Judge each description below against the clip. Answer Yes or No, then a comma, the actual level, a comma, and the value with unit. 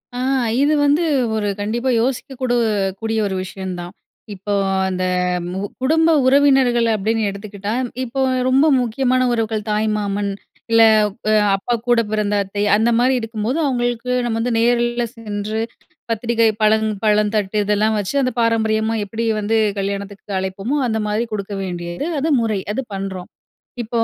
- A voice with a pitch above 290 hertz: No, high, 220 Hz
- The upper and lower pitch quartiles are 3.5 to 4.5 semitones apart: No, average, 2.9 semitones